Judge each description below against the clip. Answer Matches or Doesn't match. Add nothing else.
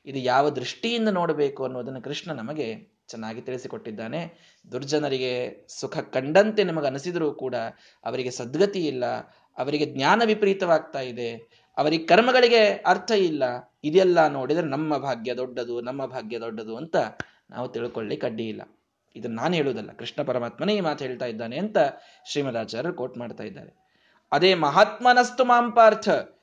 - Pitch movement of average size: Doesn't match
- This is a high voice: Doesn't match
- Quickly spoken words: Matches